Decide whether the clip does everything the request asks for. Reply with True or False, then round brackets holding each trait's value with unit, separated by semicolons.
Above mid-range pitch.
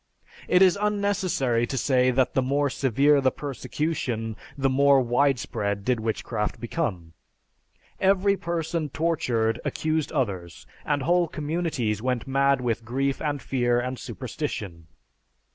False (135 Hz)